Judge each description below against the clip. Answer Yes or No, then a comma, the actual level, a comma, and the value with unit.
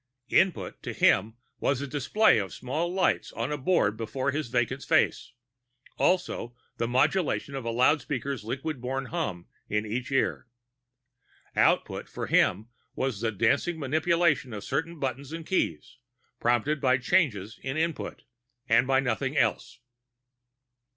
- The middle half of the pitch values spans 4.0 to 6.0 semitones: Yes, average, 4.8 semitones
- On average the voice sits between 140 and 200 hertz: No, low, 130 Hz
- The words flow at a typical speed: Yes, average, 145 wpm